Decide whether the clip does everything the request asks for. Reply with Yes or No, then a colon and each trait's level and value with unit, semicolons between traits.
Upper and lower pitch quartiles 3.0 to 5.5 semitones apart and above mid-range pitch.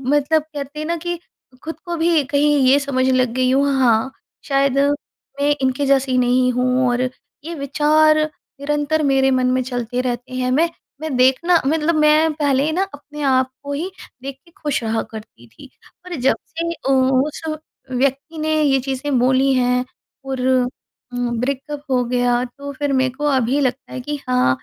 No: narrow, 2.6 semitones; very high, 270 Hz